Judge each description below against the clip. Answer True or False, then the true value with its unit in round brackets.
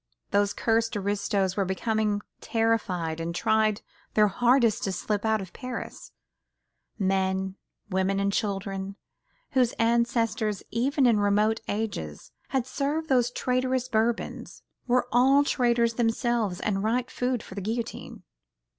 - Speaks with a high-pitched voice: True (220 Hz)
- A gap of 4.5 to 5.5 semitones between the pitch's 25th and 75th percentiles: False (3.4 semitones)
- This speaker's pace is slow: True (130 wpm)